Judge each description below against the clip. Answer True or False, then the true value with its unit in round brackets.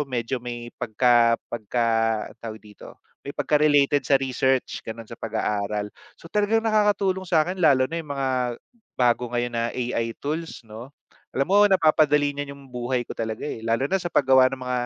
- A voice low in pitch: True (130 Hz)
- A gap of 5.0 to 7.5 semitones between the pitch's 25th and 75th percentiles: False (4.2 semitones)